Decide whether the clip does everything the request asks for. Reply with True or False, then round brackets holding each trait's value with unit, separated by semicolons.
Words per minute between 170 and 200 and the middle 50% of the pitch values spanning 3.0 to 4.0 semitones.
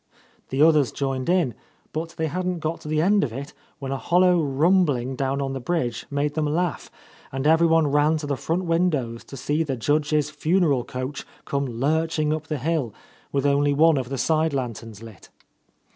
True (190 wpm; 3.3 semitones)